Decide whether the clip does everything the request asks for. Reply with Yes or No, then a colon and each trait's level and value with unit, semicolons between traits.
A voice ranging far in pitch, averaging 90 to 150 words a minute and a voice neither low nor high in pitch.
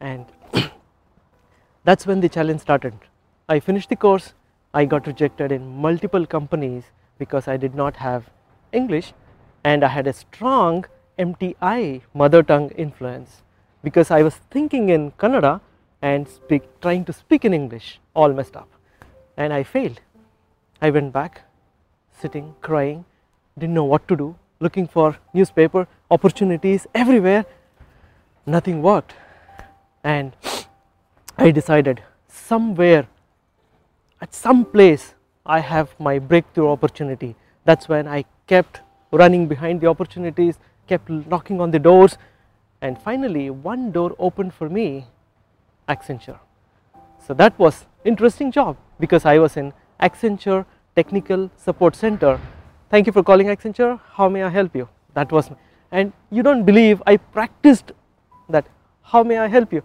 Yes: wide, 6.1 semitones; average, 140 wpm; medium, 155 Hz